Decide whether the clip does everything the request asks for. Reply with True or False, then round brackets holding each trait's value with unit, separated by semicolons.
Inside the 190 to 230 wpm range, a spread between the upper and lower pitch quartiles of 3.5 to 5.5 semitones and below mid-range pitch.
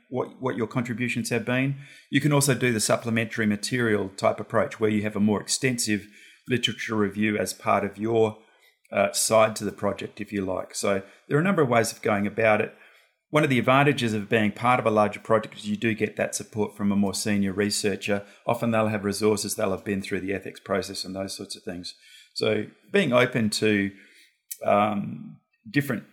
False (205 wpm; 2.9 semitones; 110 Hz)